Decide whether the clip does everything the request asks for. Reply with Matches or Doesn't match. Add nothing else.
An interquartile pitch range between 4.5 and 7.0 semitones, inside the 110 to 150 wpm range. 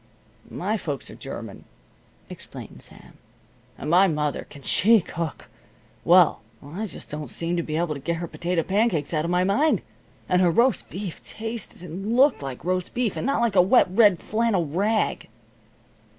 Doesn't match